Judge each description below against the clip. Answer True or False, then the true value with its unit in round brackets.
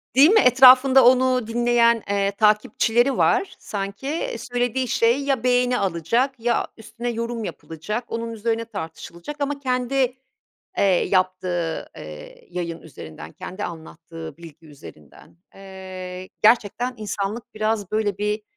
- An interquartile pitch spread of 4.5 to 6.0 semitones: True (5.2 semitones)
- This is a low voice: False (220 Hz)